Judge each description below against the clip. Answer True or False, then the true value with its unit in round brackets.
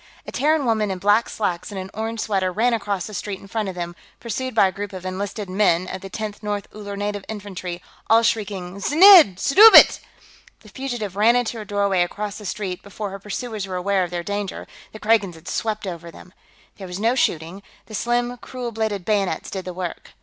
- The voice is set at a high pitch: True (205 Hz)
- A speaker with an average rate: False (210 wpm)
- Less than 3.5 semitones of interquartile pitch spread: True (2.8 semitones)